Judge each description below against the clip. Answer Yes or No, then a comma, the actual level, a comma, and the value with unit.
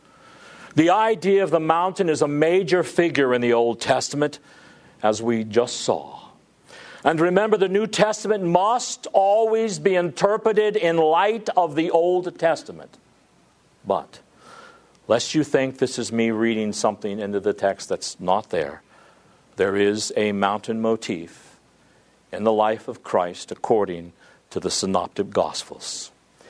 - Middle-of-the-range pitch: Yes, medium, 155 Hz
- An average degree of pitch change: No, wide, 9.0 semitones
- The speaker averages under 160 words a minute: Yes, average, 140 wpm